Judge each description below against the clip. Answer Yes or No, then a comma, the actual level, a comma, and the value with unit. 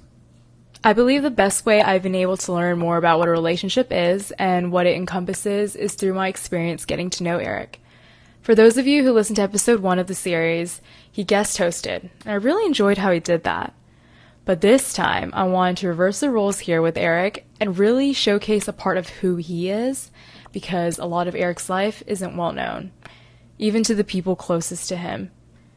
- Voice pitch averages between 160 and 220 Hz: Yes, high, 190 Hz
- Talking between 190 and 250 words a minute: Yes, fast, 205 wpm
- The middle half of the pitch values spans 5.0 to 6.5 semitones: No, average, 3.0 semitones